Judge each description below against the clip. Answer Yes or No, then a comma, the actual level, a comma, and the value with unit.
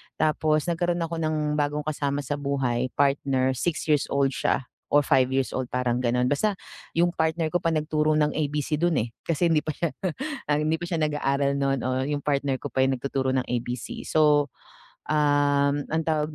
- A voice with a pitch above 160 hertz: No, medium, 145 Hz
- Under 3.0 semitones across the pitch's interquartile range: Yes, narrow, 2.5 semitones